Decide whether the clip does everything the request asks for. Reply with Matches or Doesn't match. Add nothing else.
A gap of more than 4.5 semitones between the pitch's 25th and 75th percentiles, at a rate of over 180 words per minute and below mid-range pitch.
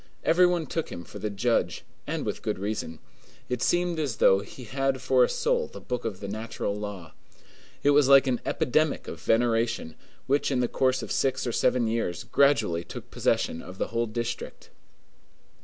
Matches